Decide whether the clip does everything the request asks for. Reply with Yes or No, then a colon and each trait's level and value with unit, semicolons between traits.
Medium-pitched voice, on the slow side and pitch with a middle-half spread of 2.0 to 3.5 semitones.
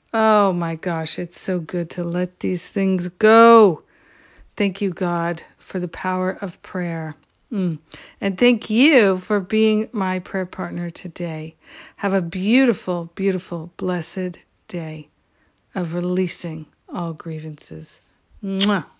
Yes: medium, 180 Hz; slow, 125 wpm; narrow, 2.5 semitones